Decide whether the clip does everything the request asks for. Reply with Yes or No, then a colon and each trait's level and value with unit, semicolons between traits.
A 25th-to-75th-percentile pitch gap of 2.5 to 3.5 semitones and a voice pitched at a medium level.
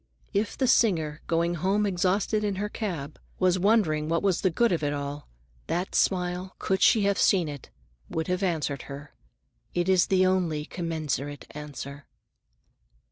No: average, 4.2 semitones; medium, 175 Hz